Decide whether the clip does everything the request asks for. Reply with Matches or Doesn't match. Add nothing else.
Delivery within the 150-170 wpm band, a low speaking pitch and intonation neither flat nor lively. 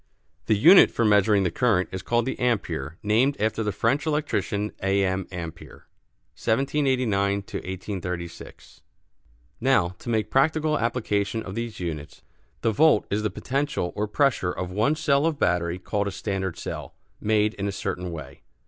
Matches